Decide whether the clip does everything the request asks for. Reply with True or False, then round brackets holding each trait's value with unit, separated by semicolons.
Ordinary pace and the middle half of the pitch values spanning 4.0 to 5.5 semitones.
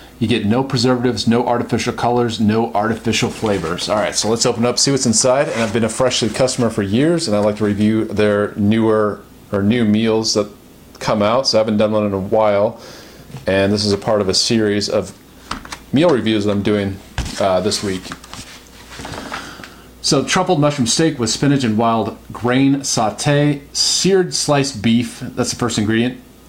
False (190 wpm; 2.8 semitones)